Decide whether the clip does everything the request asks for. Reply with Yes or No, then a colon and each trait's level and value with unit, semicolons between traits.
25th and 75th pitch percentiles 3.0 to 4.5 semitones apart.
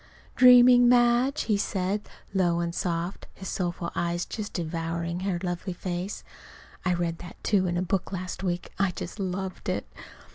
No: narrow, 2.5 semitones